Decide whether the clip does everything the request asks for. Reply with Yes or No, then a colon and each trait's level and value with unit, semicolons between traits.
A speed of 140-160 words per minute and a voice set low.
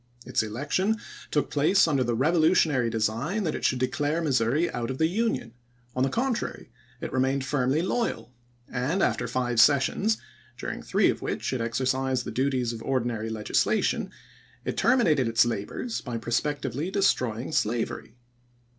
Yes: average, 150 wpm; low, 130 Hz